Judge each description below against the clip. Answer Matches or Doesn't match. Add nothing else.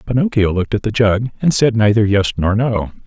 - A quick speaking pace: Matches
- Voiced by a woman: Doesn't match